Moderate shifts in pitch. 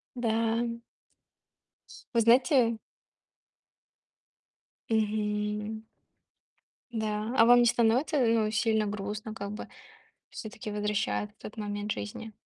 No: narrow, 1.7 semitones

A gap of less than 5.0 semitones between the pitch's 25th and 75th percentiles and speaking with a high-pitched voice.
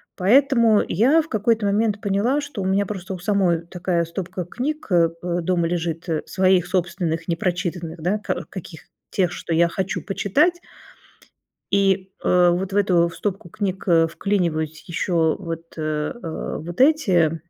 No: average, 3.2 semitones; medium, 180 Hz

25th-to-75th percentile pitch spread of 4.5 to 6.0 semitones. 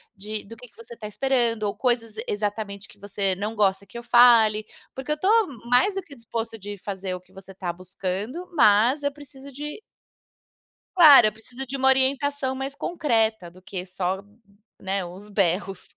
Yes: average, 5.1 semitones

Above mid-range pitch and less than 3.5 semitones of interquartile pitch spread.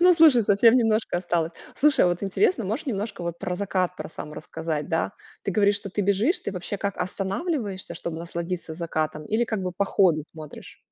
No: high, 195 Hz; average, 4.3 semitones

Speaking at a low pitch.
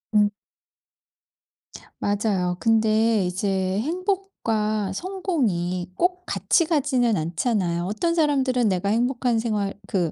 No: high, 220 Hz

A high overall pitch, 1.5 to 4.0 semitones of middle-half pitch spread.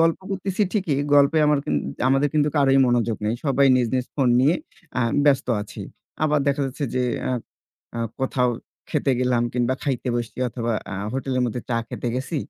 No: low, 135 Hz; average, 2.8 semitones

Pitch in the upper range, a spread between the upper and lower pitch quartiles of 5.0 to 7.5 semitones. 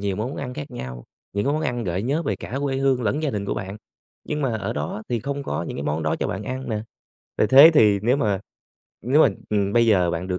No: low, 110 Hz; wide, 5.6 semitones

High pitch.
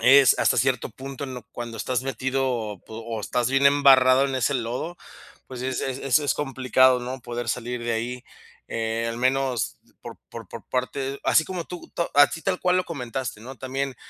No: low, 130 Hz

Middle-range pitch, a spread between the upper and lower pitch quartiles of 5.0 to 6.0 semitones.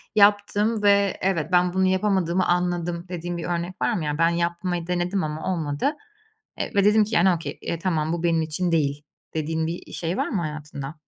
No: medium, 175 Hz; narrow, 2.6 semitones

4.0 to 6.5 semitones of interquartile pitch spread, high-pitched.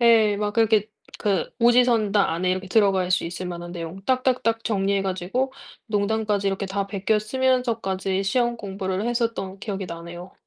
No: average, 3.2 semitones; high, 200 Hz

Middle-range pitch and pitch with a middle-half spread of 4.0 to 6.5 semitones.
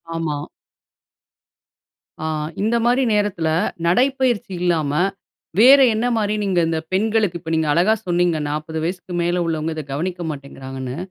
Yes: medium, 175 Hz; average, 4.9 semitones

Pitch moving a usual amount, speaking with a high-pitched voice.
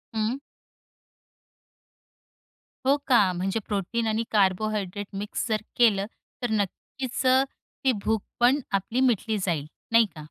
Yes: average, 3.6 semitones; high, 220 Hz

